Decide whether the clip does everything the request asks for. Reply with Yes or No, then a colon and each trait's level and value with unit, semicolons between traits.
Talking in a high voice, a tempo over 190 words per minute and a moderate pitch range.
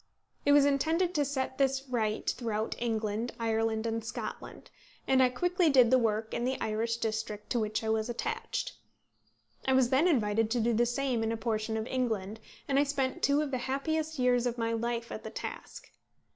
Yes: high, 240 Hz; average, 200 wpm; average, 3.3 semitones